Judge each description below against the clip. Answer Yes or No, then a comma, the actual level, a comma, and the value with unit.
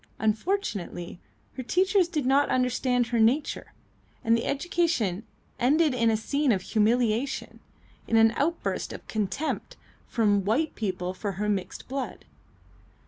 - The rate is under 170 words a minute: Yes, slow, 135 wpm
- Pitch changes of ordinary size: Yes, average, 5.0 semitones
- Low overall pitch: No, high, 235 Hz